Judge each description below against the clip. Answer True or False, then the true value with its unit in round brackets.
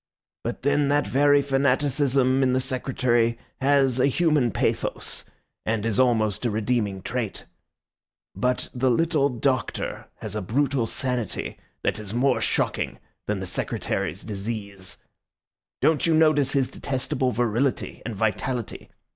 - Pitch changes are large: False (3.9 semitones)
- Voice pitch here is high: False (125 Hz)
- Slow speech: True (130 wpm)